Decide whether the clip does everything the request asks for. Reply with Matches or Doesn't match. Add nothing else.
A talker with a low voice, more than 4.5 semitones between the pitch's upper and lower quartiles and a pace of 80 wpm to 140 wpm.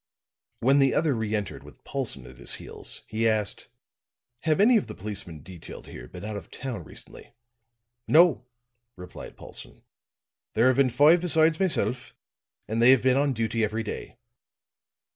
Doesn't match